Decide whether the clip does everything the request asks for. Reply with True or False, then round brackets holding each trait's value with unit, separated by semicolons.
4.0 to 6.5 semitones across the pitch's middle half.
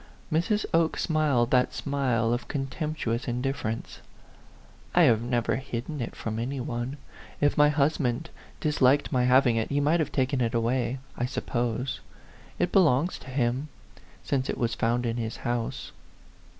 False (3.5 semitones)